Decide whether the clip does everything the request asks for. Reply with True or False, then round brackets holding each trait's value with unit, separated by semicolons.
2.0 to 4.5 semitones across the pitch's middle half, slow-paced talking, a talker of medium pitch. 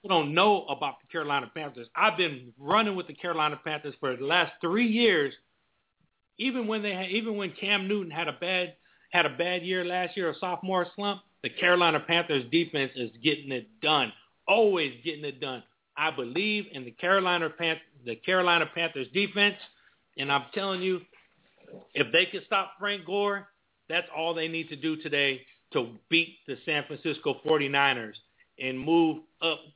False (4.2 semitones; 175 wpm; 170 Hz)